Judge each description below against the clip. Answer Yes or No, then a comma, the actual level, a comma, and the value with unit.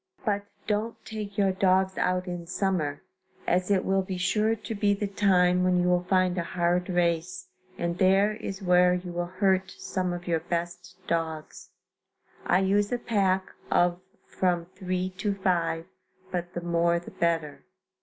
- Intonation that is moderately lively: No, narrow, 1.9 semitones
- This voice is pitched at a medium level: Yes, medium, 180 Hz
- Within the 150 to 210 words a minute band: Yes, average, 165 wpm